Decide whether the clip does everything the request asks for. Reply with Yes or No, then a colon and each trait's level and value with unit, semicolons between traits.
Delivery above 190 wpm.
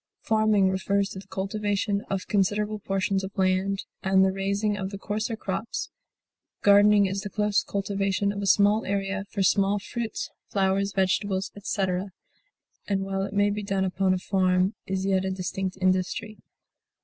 No: average, 160 wpm